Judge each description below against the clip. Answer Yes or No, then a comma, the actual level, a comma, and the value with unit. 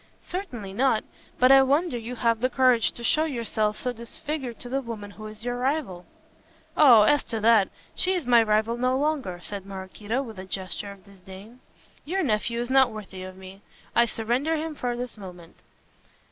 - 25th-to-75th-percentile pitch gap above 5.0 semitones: No, average, 4.3 semitones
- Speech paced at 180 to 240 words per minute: Yes, average, 190 wpm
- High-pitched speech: Yes, high, 235 Hz